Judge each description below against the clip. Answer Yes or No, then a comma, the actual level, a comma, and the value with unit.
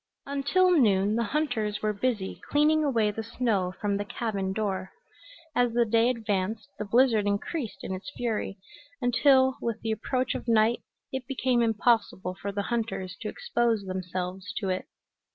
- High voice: Yes, high, 225 Hz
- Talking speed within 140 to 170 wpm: Yes, average, 160 wpm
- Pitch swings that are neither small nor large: Yes, average, 3.6 semitones